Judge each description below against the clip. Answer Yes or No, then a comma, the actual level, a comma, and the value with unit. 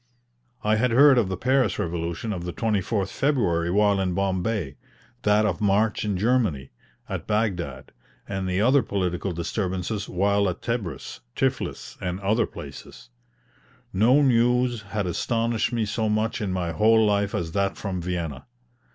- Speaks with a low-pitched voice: Yes, low, 100 Hz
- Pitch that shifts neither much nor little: Yes, average, 3.8 semitones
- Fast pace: No, average, 150 wpm